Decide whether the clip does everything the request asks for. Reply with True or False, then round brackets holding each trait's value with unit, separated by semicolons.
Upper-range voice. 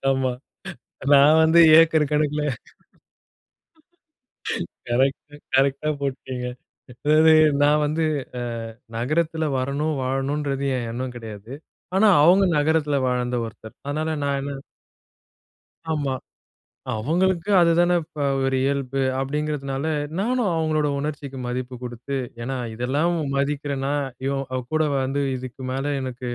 False (140 Hz)